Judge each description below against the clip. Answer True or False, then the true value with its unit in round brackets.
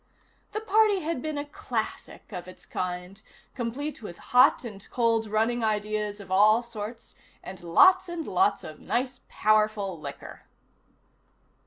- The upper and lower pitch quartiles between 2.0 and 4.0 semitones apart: False (5.0 semitones)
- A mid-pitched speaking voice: False (220 Hz)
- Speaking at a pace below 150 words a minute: True (140 wpm)